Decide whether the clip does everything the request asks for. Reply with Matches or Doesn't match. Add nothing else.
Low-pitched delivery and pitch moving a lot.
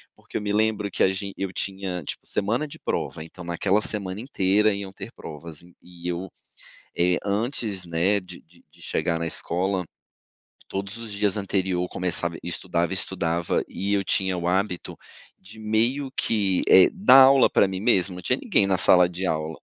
Doesn't match